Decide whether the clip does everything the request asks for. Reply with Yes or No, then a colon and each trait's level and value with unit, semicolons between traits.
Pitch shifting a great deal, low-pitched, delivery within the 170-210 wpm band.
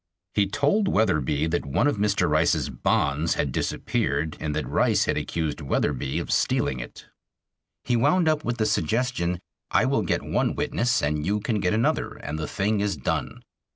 Yes: wide, 7.6 semitones; very low, 95 Hz; average, 180 wpm